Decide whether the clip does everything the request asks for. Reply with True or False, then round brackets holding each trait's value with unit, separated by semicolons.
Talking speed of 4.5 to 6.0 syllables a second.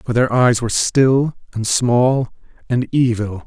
False (4.0 syllables/s)